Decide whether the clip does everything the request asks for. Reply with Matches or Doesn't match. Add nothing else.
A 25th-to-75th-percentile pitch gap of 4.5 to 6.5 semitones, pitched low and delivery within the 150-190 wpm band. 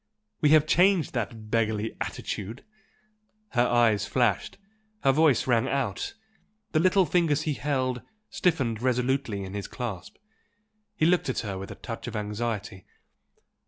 Doesn't match